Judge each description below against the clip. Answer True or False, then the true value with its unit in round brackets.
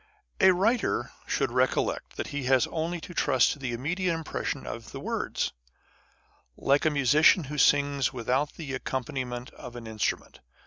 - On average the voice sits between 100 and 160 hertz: True (140 Hz)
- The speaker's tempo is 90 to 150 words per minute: False (160 wpm)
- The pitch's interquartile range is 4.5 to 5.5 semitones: False (4.0 semitones)